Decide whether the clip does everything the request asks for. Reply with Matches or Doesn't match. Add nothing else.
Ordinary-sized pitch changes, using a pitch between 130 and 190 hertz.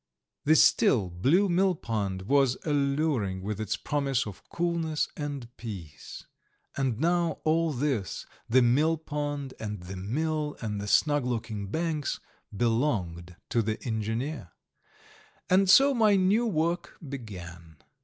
Doesn't match